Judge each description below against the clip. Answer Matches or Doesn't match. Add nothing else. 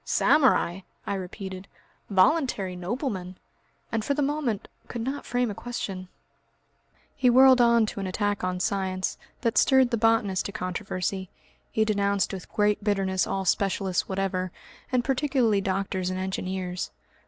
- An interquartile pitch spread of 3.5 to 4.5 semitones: Matches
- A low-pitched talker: Doesn't match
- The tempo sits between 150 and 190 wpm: Doesn't match